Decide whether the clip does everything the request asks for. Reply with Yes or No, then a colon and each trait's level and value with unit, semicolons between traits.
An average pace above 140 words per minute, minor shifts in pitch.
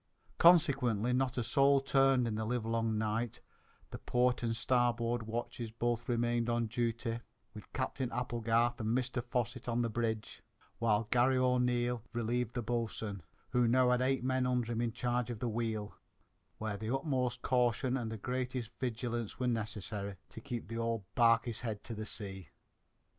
Yes: average, 165 wpm; narrow, 1.6 semitones